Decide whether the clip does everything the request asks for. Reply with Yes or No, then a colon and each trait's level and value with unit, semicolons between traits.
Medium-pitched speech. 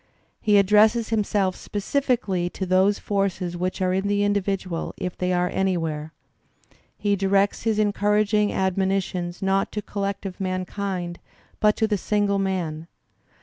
No: high, 195 Hz